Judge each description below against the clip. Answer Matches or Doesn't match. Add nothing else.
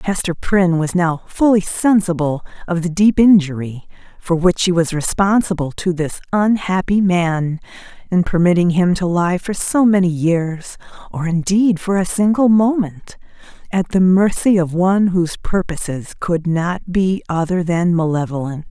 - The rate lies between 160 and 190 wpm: Doesn't match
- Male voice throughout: Doesn't match